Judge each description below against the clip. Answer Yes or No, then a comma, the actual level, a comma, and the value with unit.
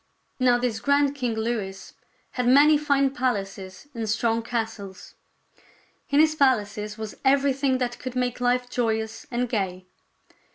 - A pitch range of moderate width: Yes, average, 3.3 semitones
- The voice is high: Yes, high, 245 Hz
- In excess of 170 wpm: No, slow, 135 wpm